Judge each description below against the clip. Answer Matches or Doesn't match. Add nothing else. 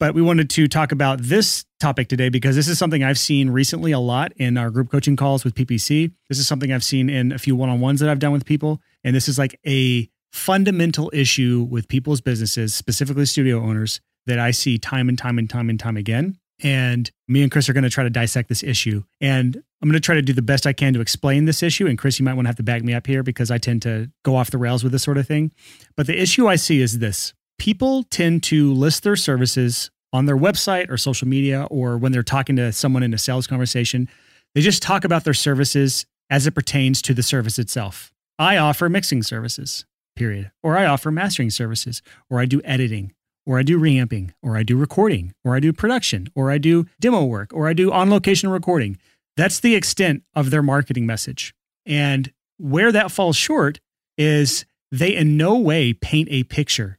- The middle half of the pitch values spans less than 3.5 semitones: Doesn't match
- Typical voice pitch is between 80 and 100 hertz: Doesn't match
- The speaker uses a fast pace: Matches